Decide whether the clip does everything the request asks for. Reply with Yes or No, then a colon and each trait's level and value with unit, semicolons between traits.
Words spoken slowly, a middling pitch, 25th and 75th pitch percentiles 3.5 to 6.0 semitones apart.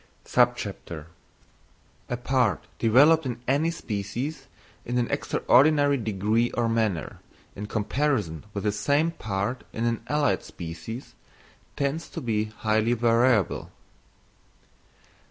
No: slow, 100 wpm; low, 115 Hz; average, 4.5 semitones